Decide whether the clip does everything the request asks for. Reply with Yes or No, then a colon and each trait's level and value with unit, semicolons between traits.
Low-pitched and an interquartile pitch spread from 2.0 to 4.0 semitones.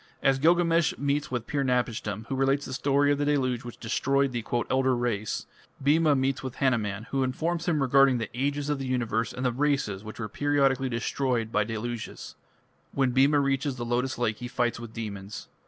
Yes: low, 130 Hz; average, 3.0 semitones